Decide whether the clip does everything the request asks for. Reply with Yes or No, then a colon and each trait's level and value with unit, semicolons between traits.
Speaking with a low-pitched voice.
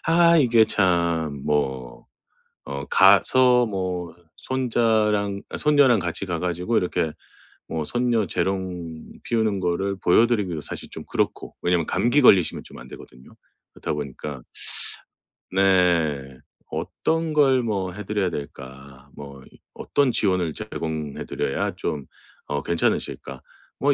Yes: very low, 90 Hz